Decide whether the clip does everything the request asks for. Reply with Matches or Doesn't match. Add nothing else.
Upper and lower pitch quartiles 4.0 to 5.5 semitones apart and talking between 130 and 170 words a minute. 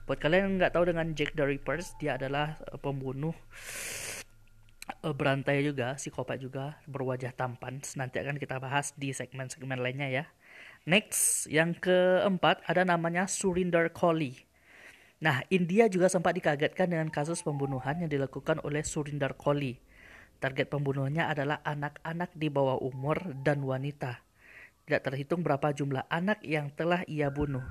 Doesn't match